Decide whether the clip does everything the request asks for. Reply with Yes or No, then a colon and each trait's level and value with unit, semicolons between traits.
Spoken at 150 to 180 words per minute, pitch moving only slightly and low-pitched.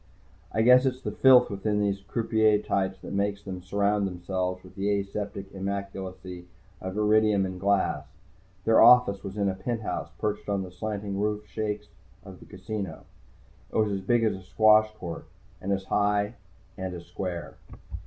Yes: average, 165 wpm; narrow, 2.0 semitones; low, 100 Hz